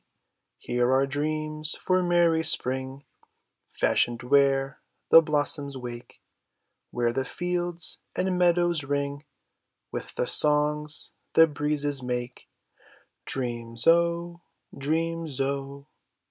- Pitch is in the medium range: Yes, medium, 145 Hz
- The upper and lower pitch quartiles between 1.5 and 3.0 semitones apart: No, average, 3.5 semitones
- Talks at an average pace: No, slow, 100 wpm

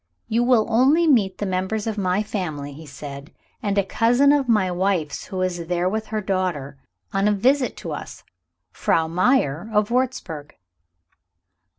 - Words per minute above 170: No, average, 165 wpm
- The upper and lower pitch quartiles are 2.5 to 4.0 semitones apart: No, average, 4.5 semitones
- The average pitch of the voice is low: No, high, 195 Hz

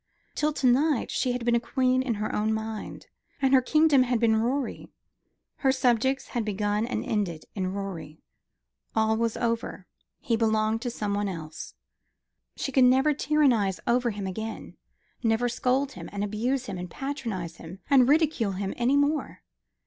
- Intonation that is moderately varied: Yes, average, 4.0 semitones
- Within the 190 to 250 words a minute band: No, average, 170 wpm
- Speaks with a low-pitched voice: No, high, 230 Hz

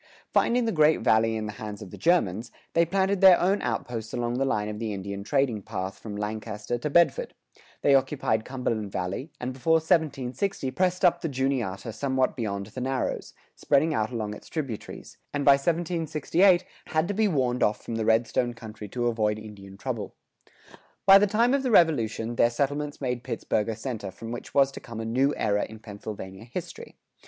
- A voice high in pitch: No, low, 125 Hz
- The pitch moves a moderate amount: No, wide, 6.4 semitones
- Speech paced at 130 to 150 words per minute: No, average, 190 wpm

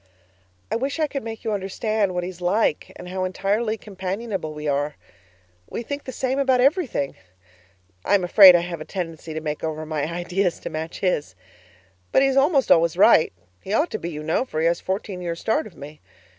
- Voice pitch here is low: No, medium, 185 Hz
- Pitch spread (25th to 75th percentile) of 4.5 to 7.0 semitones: Yes, wide, 5.6 semitones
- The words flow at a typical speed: No, fast, 210 wpm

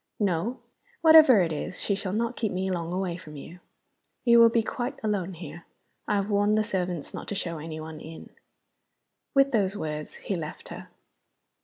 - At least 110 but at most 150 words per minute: No, average, 185 wpm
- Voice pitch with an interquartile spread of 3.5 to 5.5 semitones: Yes, average, 4.6 semitones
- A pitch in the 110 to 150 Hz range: No, high, 190 Hz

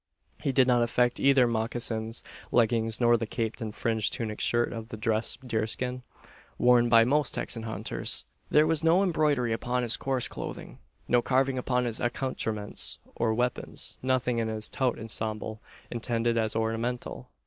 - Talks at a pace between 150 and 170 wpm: Yes, average, 155 wpm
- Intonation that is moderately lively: No, narrow, 2.1 semitones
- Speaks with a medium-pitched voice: No, low, 120 Hz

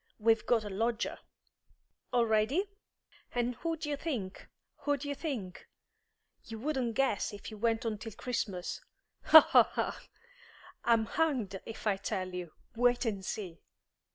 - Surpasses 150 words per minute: No, average, 140 wpm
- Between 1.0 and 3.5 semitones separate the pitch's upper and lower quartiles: No, average, 4.0 semitones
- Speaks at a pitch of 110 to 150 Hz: No, high, 225 Hz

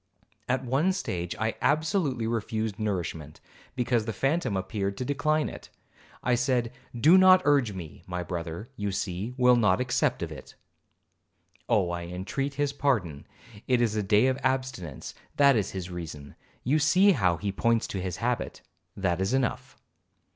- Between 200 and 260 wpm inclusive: No, average, 155 wpm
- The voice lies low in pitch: Yes, low, 115 Hz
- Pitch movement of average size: No, wide, 6.3 semitones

